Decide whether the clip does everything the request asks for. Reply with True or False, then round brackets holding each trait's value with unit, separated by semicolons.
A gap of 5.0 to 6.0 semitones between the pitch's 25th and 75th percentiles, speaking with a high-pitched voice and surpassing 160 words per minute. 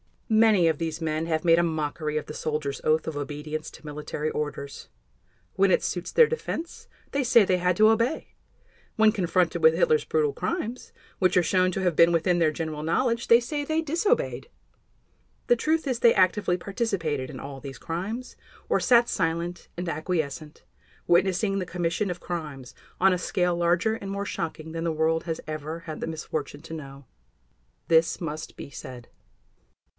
False (5.3 semitones; 170 Hz; 180 wpm)